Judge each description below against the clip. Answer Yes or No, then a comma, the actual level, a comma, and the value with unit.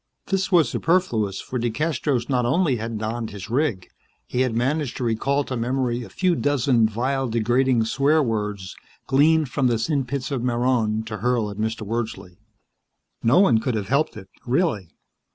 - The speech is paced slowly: No, average, 170 wpm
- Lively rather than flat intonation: No, average, 3.8 semitones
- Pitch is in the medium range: No, low, 120 Hz